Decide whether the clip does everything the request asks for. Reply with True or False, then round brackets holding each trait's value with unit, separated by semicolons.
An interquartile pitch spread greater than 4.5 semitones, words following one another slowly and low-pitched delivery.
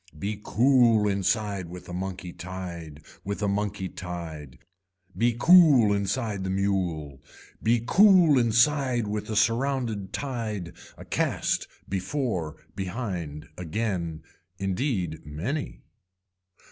True (5.0 semitones; 110 wpm; 100 Hz)